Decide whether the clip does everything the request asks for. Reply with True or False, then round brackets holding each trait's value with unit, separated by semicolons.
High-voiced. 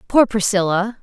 True (210 Hz)